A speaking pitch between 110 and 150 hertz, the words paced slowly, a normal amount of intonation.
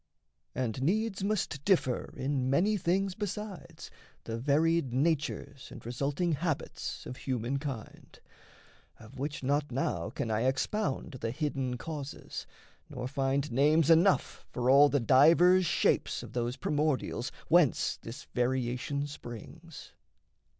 Yes: medium, 140 Hz; slow, 120 wpm; average, 4.5 semitones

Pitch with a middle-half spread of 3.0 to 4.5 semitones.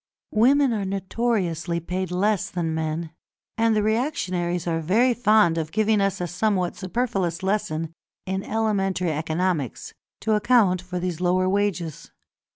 Yes: average, 3.8 semitones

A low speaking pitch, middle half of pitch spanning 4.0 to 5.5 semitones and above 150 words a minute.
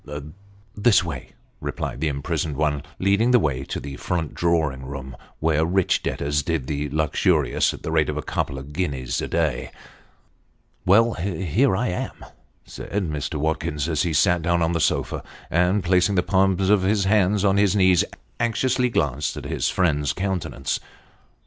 Yes: very low, 85 Hz; average, 4.7 semitones; average, 175 wpm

